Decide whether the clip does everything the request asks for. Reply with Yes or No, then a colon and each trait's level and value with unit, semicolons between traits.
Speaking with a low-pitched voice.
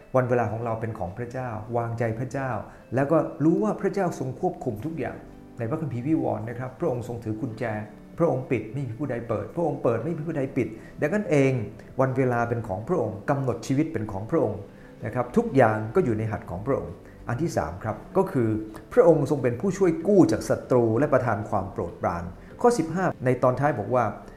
Yes: low, 125 Hz